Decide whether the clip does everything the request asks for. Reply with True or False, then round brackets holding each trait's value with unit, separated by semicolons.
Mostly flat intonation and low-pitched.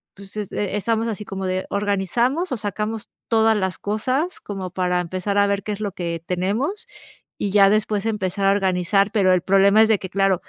False (2.3 semitones; 200 Hz)